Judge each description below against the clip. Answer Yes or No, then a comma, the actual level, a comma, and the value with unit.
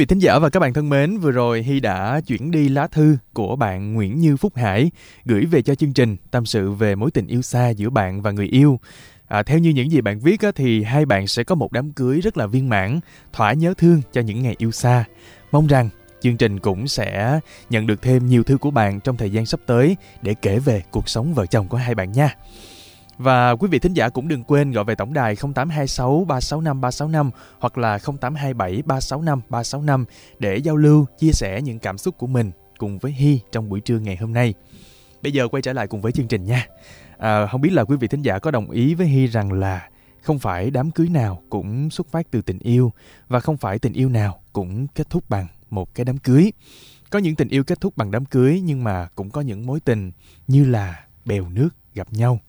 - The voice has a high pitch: No, low, 125 Hz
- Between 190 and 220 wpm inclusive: No, average, 235 wpm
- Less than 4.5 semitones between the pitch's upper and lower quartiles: No, average, 5.1 semitones